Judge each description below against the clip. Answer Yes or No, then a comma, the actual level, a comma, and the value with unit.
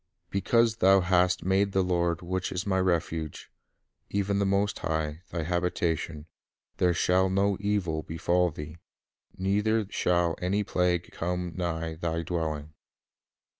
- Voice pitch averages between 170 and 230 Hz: No, very low, 90 Hz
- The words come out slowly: Yes, slow, 130 wpm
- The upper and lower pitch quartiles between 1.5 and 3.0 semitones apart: Yes, average, 2.7 semitones